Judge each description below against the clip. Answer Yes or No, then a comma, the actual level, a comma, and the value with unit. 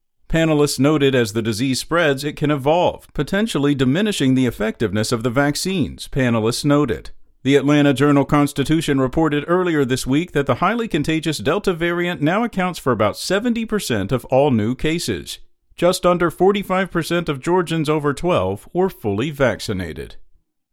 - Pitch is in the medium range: Yes, medium, 145 Hz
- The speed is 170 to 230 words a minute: No, average, 145 wpm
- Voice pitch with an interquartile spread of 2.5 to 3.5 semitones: No, average, 4.9 semitones